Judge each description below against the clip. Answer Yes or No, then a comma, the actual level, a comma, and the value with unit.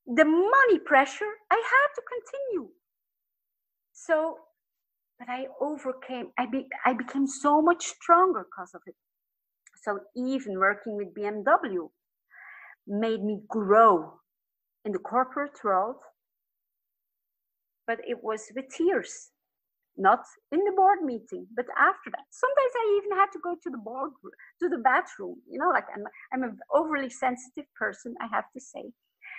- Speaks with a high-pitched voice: Yes, very high, 280 Hz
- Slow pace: No, average, 145 wpm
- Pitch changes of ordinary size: No, wide, 6.4 semitones